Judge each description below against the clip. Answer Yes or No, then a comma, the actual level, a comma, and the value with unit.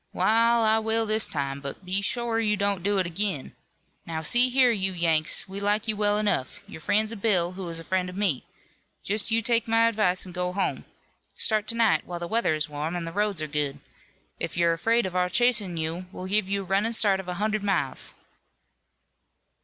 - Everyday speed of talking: No, fast, 215 wpm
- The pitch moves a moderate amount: Yes, average, 4.0 semitones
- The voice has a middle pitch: No, high, 195 Hz